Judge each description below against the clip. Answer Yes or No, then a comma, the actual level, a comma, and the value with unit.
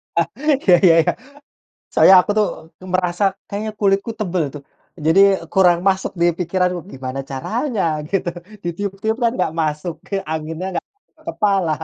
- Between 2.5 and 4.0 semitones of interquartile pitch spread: Yes, average, 3.2 semitones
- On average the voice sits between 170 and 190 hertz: Yes, medium, 185 Hz